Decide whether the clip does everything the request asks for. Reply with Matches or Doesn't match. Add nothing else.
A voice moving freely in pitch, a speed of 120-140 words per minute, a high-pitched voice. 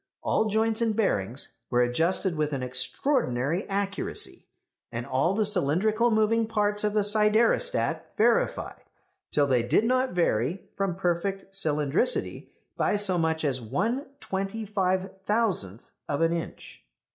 Matches